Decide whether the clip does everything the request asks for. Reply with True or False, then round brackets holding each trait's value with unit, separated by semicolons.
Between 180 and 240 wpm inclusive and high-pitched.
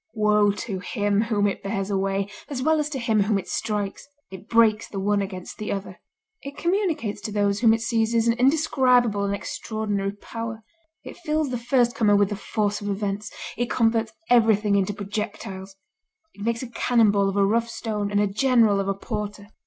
True (190 wpm; 210 Hz)